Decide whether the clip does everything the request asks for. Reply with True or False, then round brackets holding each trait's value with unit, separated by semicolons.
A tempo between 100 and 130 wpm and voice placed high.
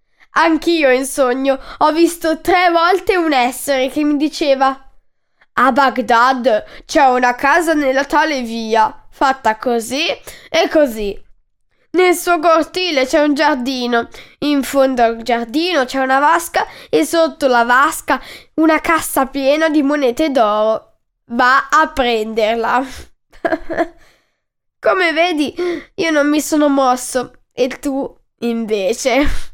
True (120 wpm; 275 Hz)